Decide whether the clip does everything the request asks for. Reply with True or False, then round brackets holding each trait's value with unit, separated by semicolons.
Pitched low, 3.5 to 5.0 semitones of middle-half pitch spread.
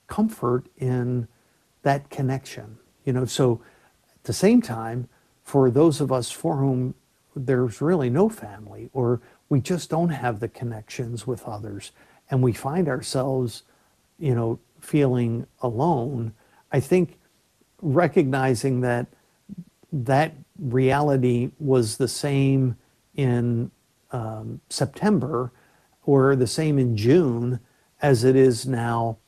False (130 Hz; 3.0 semitones)